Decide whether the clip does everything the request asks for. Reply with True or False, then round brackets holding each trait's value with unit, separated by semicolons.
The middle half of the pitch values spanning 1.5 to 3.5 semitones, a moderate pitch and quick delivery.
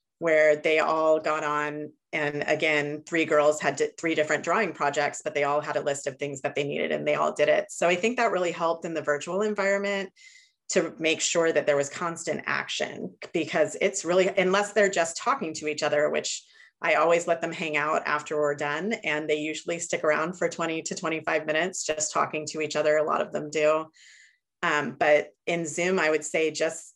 True (2.4 semitones; 155 Hz; 215 wpm)